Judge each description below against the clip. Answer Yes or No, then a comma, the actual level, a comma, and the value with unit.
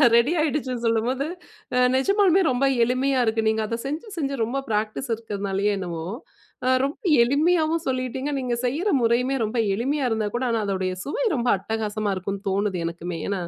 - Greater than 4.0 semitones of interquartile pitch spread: Yes, average, 4.7 semitones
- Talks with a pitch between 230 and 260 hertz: Yes, high, 240 Hz